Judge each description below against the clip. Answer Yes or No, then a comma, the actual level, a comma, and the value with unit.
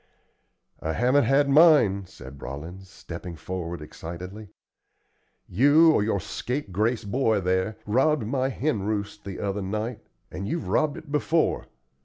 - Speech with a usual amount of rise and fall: No, wide, 6.6 semitones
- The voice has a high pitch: No, low, 105 Hz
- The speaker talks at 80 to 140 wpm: Yes, slow, 135 wpm